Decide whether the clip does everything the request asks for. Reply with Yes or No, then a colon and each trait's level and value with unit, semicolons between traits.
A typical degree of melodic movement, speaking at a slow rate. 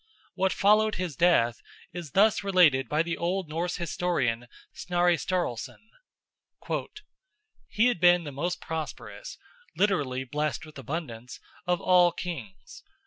Yes: average, 4.1 semitones; slow, 125 wpm